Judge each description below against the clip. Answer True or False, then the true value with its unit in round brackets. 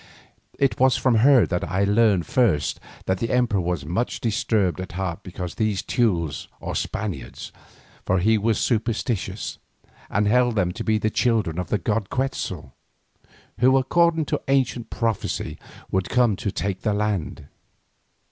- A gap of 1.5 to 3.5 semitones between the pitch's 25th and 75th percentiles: False (4.6 semitones)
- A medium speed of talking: True (155 wpm)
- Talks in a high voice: False (105 Hz)